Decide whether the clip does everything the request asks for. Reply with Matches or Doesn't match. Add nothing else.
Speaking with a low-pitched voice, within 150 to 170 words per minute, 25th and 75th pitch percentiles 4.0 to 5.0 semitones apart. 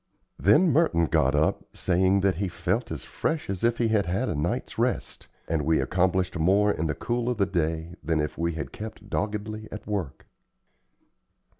Doesn't match